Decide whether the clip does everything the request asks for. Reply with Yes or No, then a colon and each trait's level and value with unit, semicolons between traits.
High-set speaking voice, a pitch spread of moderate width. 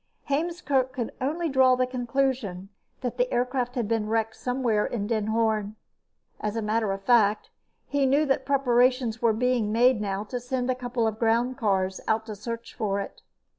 Yes: high, 240 Hz; average, 3.0 semitones